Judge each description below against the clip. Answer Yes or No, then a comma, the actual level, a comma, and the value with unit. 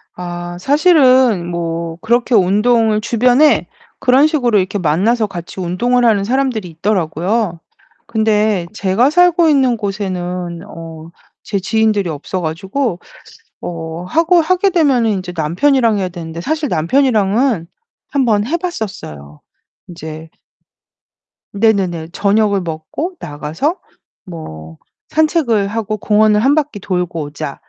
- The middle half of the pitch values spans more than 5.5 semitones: Yes, wide, 6.4 semitones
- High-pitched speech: Yes, high, 205 Hz